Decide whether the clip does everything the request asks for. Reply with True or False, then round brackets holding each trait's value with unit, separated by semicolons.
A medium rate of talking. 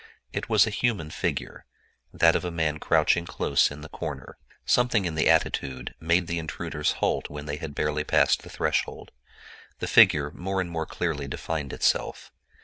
True (170 wpm)